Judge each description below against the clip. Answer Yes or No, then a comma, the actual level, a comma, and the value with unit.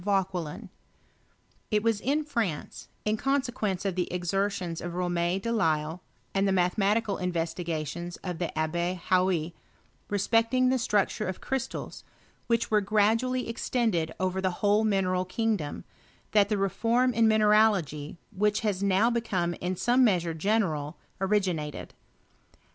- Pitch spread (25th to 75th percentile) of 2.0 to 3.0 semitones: No, average, 3.9 semitones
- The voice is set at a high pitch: Yes, high, 195 Hz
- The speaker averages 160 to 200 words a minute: No, slow, 135 wpm